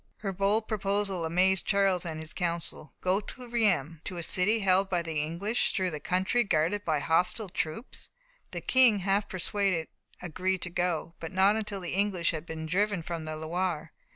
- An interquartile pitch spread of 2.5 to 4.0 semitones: Yes, average, 3.4 semitones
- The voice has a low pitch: No, medium, 185 Hz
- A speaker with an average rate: Yes, average, 180 wpm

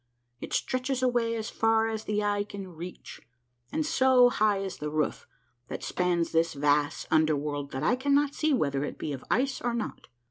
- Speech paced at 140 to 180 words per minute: No, average, 190 wpm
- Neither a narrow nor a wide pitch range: No, wide, 8.1 semitones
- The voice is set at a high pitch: Yes, high, 205 Hz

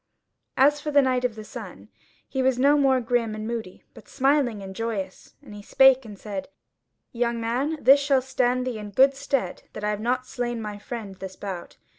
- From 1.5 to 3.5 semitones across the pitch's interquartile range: No, average, 3.9 semitones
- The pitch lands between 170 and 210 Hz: No, high, 240 Hz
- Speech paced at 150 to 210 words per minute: Yes, fast, 205 wpm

